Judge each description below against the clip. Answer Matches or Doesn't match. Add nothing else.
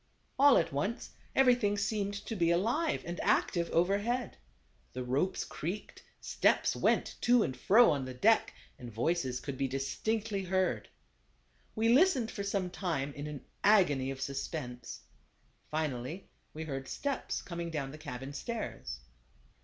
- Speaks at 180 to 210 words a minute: Doesn't match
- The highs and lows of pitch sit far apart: Matches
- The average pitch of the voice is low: Doesn't match